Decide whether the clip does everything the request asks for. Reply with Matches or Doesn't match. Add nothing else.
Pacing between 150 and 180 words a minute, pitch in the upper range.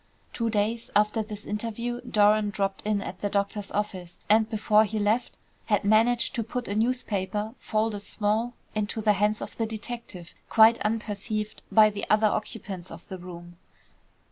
Matches